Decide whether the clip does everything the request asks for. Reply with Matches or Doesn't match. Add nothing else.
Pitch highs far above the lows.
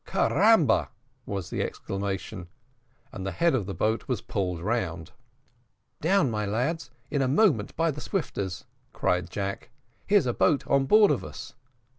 Matches